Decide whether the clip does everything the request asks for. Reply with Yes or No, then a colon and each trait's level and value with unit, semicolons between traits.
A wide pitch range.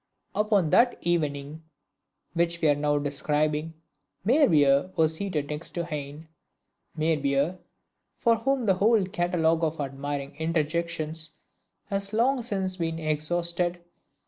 No: average, 3.7 semitones